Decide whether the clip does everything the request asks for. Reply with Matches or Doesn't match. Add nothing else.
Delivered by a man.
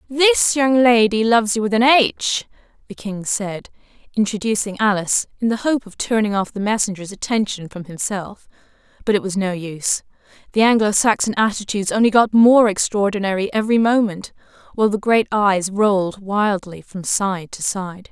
Doesn't match